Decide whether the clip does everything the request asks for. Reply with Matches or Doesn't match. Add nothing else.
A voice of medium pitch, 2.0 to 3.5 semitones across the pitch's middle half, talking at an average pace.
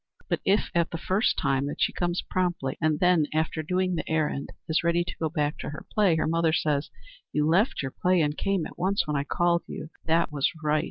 Doesn't match